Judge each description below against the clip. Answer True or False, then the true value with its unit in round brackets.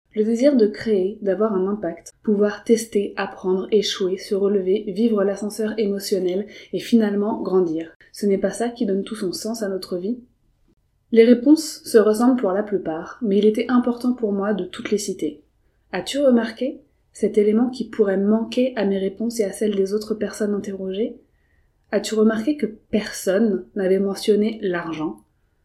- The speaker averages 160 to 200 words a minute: True (175 wpm)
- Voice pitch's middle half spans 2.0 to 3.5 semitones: True (2.6 semitones)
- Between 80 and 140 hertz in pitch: False (210 Hz)